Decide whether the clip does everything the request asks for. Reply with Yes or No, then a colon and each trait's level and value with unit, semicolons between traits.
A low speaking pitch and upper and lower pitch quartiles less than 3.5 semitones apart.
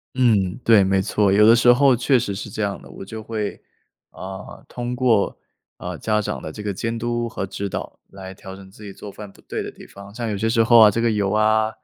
Yes: low, 105 Hz; average, 2.8 semitones